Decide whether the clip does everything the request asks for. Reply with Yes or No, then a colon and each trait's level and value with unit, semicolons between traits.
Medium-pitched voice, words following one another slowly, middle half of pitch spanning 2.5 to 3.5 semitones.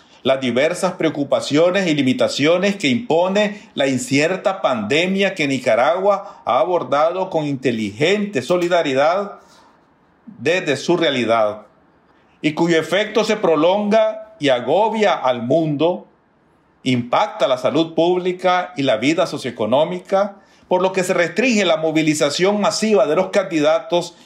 No: medium, 175 Hz; slow, 120 wpm; wide, 5.4 semitones